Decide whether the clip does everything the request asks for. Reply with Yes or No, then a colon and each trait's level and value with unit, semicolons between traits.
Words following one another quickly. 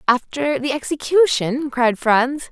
No: slow, 120 wpm